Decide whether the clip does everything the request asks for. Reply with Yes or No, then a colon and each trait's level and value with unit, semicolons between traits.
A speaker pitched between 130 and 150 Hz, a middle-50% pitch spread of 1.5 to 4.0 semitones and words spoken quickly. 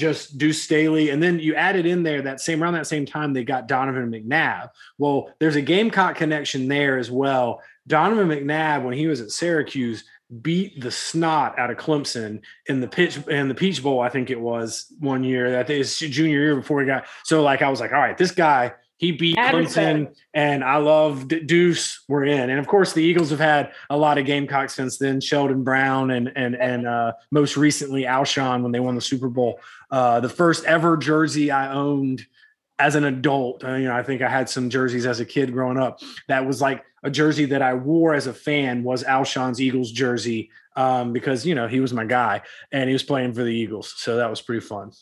Yes: medium, 140 Hz; average, 3.3 semitones; fast, 225 wpm